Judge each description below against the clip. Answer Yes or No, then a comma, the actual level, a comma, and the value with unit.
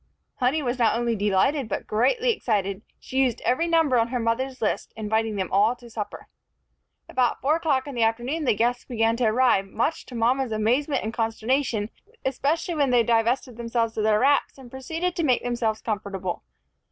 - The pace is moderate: Yes, average, 185 wpm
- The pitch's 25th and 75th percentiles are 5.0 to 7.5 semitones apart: No, average, 3.2 semitones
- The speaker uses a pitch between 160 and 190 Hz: No, high, 240 Hz